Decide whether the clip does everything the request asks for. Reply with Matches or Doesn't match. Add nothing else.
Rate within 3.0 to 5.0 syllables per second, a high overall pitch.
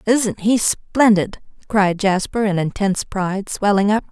Matches